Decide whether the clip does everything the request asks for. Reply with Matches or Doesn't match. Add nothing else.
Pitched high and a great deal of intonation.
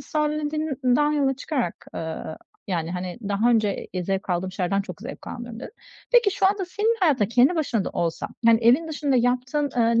Matches